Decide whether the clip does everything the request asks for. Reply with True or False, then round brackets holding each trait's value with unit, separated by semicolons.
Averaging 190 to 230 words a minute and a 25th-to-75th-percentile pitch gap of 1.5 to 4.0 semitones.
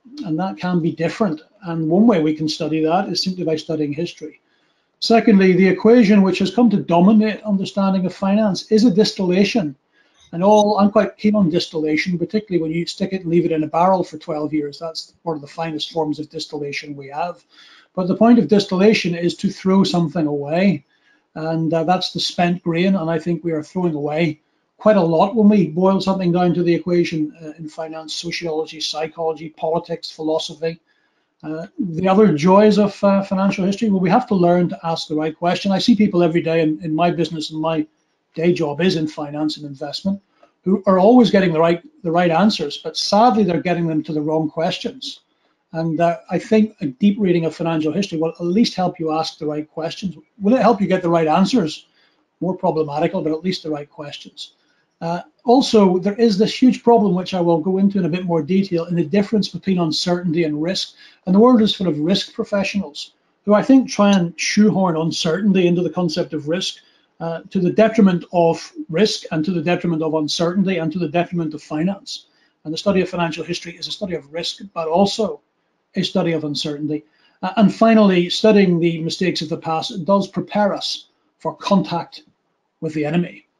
True (205 wpm; 3.5 semitones)